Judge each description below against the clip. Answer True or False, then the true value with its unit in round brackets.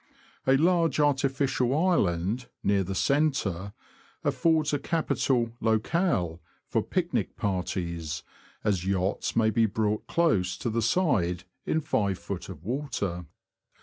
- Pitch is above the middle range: False (110 Hz)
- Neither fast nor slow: False (115 wpm)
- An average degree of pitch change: False (7.6 semitones)